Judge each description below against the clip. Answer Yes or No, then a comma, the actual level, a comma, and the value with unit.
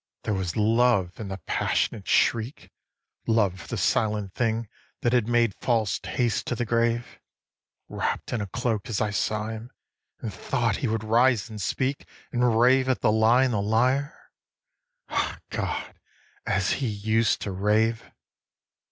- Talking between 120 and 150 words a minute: No, average, 160 wpm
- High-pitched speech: No, low, 110 Hz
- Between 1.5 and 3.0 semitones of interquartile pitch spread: Yes, narrow, 2.4 semitones